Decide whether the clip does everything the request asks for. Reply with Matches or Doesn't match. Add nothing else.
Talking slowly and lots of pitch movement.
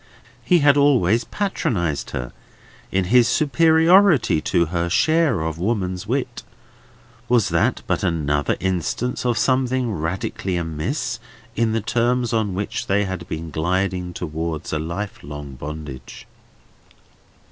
Matches